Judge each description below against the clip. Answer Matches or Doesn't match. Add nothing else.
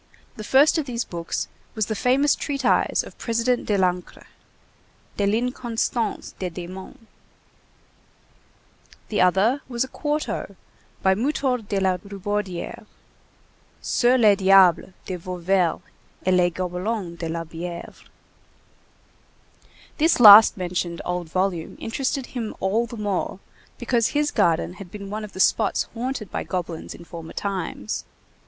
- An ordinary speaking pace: Doesn't match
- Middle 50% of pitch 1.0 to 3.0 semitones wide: Doesn't match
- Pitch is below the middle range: Doesn't match